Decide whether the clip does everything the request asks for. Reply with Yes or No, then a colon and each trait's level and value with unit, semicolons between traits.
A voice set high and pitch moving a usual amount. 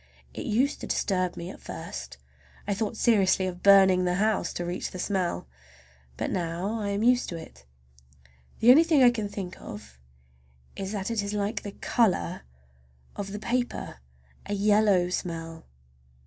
Yes: high, 195 Hz; average, 3.3 semitones